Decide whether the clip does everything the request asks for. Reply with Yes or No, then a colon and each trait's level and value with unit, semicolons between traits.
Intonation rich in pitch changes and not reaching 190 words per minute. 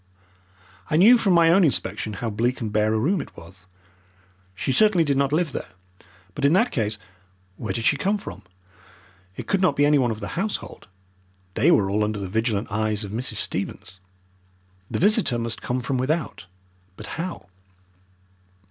Yes: wide, 7.6 semitones; average, 175 wpm